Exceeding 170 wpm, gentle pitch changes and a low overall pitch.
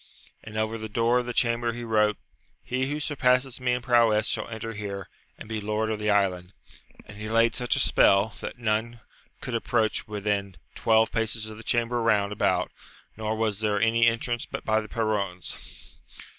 Yes: average, 185 wpm; narrow, 1.8 semitones; low, 110 Hz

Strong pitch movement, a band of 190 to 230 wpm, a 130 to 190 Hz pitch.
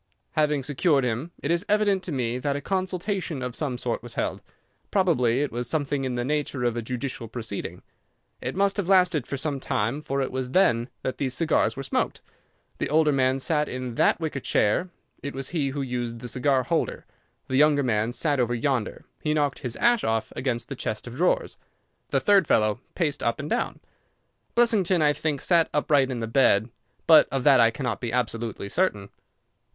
No: average, 4.4 semitones; average, 200 wpm; low, 135 Hz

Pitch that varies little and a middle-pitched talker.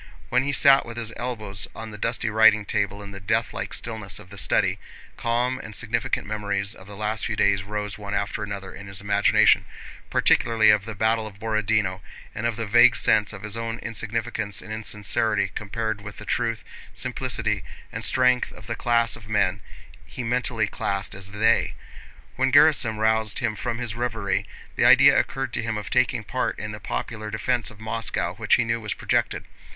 No: narrow, 2.2 semitones; low, 110 Hz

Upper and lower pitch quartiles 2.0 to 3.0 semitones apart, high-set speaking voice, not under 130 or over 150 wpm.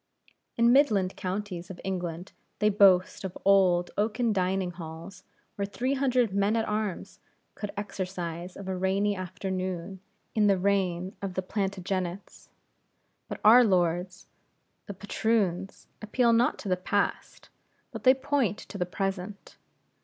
Yes: narrow, 2.5 semitones; high, 195 Hz; average, 140 wpm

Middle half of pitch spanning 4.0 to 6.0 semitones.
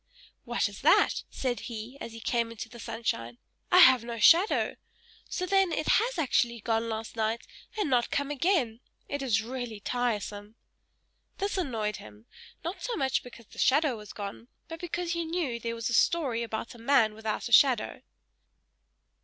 Yes: average, 5.3 semitones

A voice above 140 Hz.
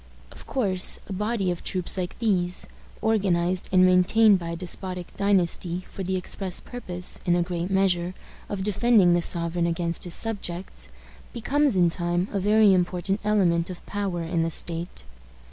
Yes: medium, 185 Hz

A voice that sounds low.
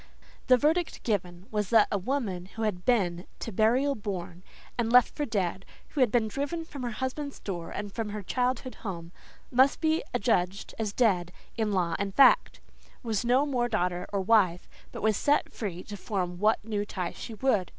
No: high, 215 Hz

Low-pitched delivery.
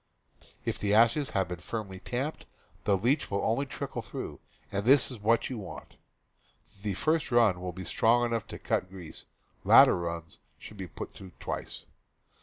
Yes: low, 105 Hz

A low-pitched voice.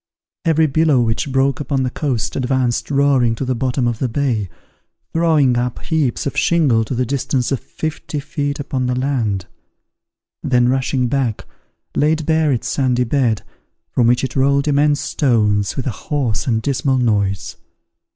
Yes: low, 130 Hz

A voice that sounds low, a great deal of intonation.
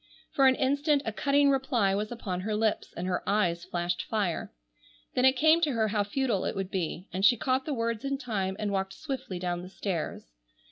No: high, 215 Hz; wide, 5.8 semitones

